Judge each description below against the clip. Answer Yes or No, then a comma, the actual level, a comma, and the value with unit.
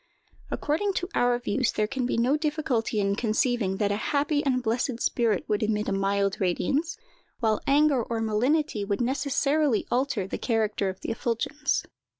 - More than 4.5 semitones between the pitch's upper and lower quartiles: Yes, average, 5.0 semitones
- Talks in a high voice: Yes, high, 235 Hz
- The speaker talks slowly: No, average, 165 wpm